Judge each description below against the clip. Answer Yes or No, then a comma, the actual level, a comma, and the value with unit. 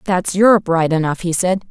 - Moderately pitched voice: Yes, medium, 180 Hz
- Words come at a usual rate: No, fast, 210 wpm